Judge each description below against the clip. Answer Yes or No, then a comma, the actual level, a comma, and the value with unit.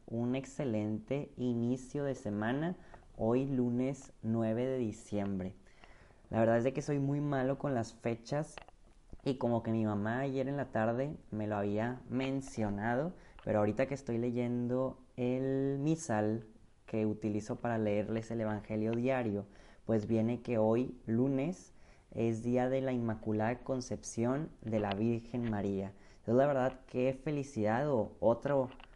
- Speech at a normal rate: Yes, average, 145 wpm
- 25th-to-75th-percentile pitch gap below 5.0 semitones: Yes, average, 3.5 semitones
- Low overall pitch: Yes, low, 120 Hz